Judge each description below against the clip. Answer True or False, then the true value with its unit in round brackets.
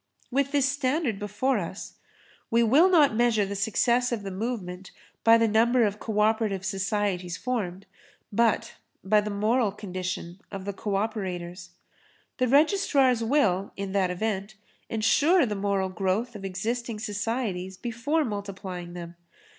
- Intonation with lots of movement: False (3.8 semitones)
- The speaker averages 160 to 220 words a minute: False (145 wpm)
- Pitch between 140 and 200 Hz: False (210 Hz)